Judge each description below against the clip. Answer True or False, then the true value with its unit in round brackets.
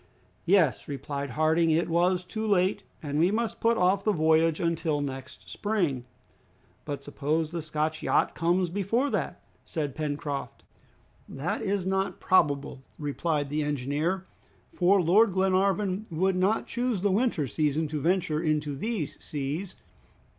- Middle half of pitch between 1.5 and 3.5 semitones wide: False (4.4 semitones)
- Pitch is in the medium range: True (165 Hz)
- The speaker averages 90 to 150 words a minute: True (140 wpm)